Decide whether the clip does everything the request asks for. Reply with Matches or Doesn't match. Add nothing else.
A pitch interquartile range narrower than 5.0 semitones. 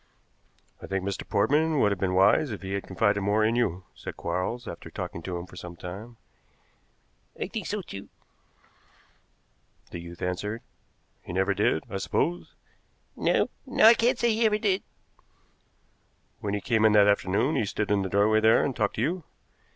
Doesn't match